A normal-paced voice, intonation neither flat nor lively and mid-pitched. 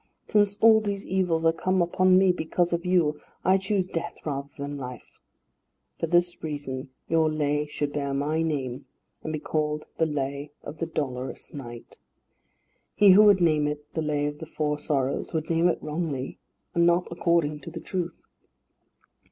Yes: average, 175 wpm; average, 3.1 semitones; medium, 155 Hz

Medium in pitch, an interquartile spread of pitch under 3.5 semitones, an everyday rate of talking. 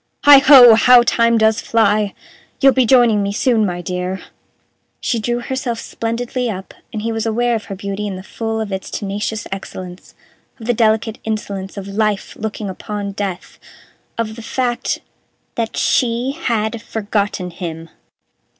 No: high, 220 Hz; average, 2.8 semitones; average, 155 wpm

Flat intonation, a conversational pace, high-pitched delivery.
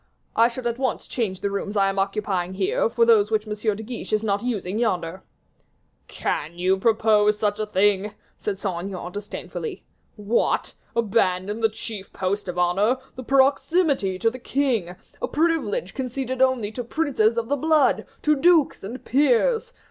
No: average, 4.5 semitones; average, 170 wpm; high, 215 Hz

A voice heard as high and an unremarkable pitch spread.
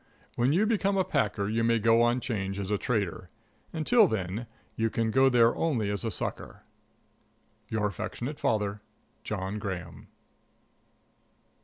No: low, 115 Hz; average, 3.6 semitones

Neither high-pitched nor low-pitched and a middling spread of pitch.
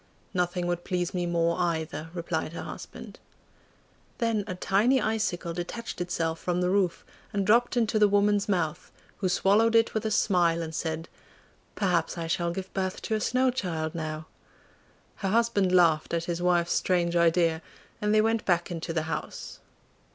Yes: medium, 180 Hz; average, 3.6 semitones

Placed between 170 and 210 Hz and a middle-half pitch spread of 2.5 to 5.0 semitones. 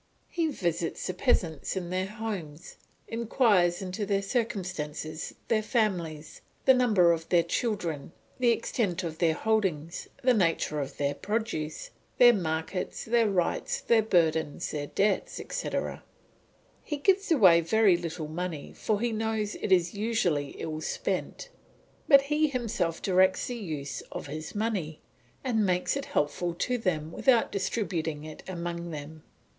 No: medium, 185 Hz; wide, 5.6 semitones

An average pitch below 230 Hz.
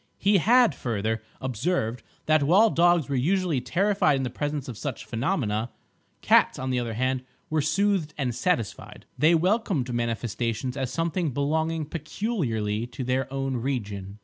Yes: low, 135 Hz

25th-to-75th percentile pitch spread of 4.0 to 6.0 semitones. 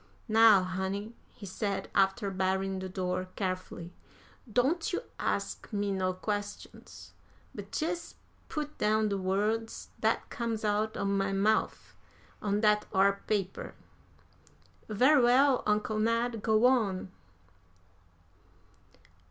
No: average, 2.7 semitones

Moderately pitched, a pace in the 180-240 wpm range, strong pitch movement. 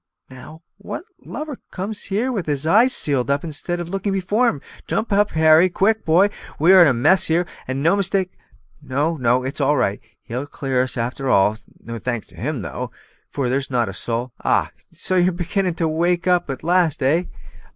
Yes: medium, 160 Hz; average, 200 wpm; wide, 6.0 semitones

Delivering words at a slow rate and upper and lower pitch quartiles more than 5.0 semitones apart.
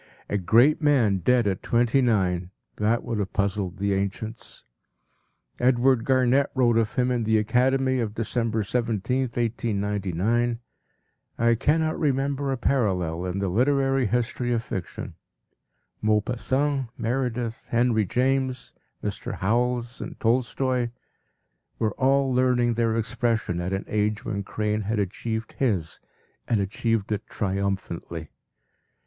No: slow, 125 wpm; average, 3.6 semitones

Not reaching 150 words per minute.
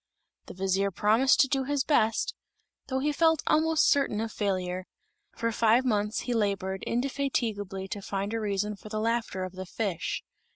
No: average, 170 wpm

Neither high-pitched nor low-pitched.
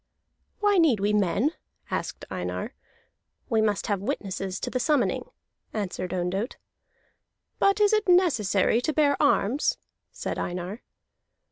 No: high, 225 Hz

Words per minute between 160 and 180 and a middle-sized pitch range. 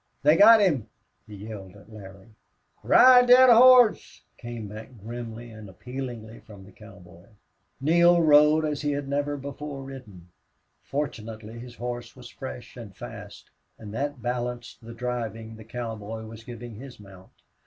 No: average, 150 wpm; average, 4.9 semitones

